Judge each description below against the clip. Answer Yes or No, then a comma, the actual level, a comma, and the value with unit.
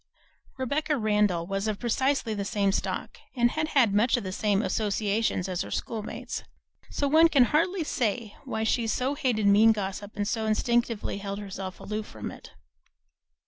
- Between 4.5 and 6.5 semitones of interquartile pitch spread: No, average, 3.7 semitones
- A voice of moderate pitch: No, high, 220 Hz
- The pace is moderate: Yes, average, 165 wpm